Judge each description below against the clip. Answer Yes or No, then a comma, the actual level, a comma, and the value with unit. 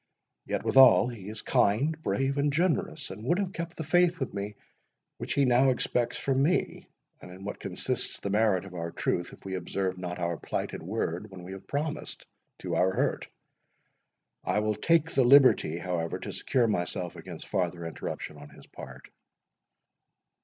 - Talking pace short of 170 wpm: No, average, 175 wpm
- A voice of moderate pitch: No, low, 105 Hz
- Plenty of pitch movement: Yes, wide, 7.4 semitones